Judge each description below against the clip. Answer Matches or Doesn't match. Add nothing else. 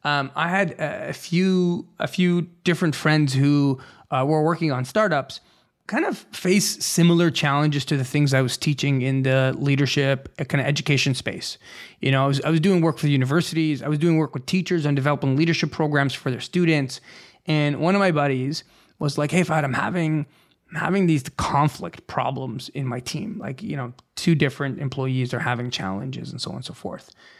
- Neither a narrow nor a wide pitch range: Matches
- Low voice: Doesn't match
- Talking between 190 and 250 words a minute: Matches